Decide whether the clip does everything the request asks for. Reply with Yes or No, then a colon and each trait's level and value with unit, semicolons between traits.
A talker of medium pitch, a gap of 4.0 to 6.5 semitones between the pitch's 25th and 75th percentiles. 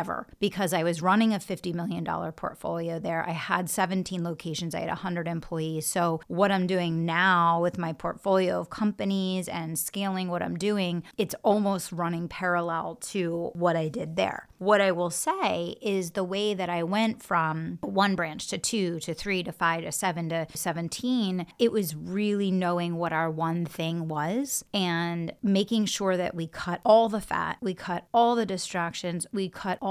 No: medium, 180 Hz; average, 2.8 semitones